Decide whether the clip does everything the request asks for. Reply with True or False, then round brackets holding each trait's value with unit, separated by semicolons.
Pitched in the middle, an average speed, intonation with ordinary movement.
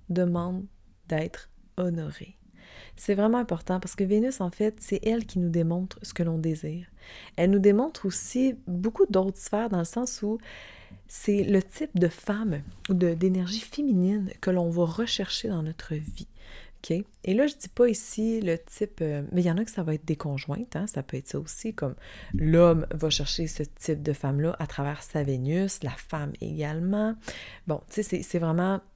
True (180 Hz; 195 wpm; 4.4 semitones)